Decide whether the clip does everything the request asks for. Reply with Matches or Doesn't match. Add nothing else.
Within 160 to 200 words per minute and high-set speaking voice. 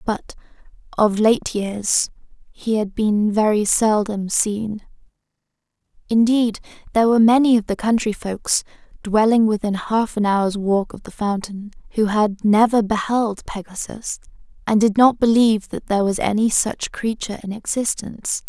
Doesn't match